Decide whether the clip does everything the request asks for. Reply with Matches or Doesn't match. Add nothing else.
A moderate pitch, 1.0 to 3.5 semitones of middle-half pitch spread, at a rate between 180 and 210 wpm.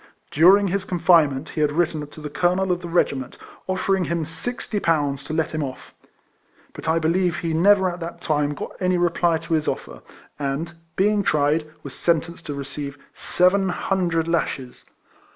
Doesn't match